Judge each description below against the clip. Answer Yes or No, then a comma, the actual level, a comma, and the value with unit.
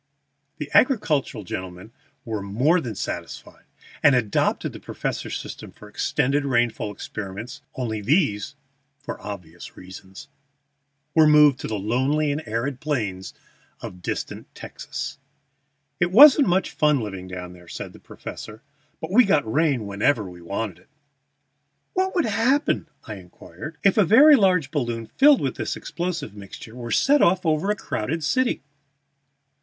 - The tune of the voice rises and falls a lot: Yes, wide, 8.0 semitones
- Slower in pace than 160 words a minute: Yes, average, 145 wpm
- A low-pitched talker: Yes, low, 130 Hz